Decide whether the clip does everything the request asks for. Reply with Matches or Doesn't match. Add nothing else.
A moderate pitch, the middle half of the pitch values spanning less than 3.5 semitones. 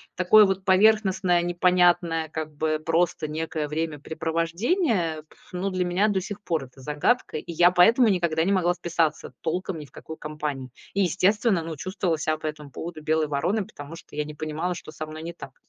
Matches